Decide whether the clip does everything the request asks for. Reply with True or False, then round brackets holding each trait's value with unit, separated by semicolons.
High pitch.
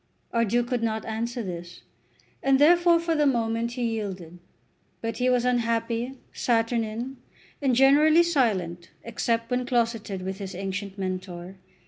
True (230 Hz)